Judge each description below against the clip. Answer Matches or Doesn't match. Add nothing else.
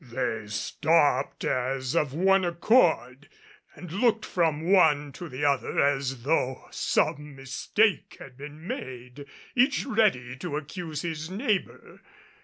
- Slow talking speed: Matches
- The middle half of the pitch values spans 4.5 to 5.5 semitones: Matches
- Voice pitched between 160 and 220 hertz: Doesn't match